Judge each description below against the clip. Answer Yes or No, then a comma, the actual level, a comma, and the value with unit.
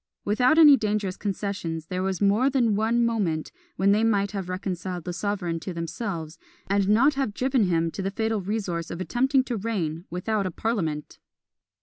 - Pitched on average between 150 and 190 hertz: No, high, 200 Hz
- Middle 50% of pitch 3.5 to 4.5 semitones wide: Yes, average, 4.0 semitones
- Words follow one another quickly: No, average, 180 wpm